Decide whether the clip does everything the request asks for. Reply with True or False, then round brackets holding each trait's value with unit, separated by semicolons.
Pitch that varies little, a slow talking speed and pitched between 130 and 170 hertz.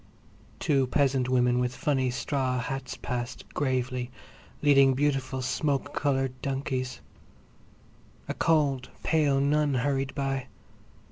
True (1.8 semitones; 110 wpm; 135 Hz)